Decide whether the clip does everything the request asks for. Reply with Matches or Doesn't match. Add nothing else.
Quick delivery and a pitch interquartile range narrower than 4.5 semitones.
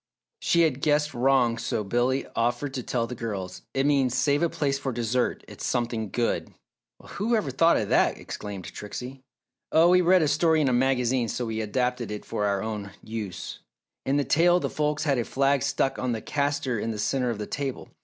Matches